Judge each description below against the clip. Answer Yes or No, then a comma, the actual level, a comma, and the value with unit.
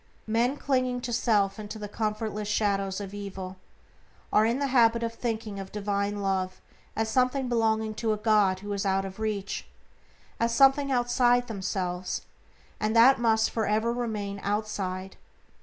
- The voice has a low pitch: No, high, 215 Hz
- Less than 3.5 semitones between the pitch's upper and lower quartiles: Yes, average, 2.8 semitones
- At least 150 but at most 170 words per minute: Yes, average, 160 wpm